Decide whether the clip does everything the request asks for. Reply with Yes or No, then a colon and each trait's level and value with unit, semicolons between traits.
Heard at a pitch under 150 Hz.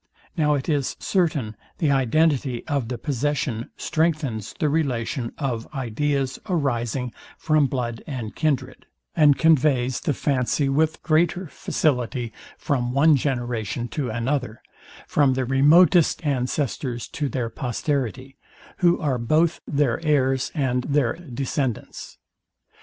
Yes: low, 135 Hz